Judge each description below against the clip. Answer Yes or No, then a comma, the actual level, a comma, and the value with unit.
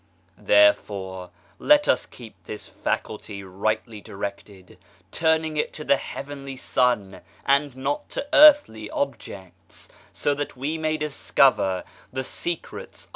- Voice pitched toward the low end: Yes, low, 130 Hz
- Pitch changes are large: Yes, wide, 6.7 semitones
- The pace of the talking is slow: Yes, slow, 120 wpm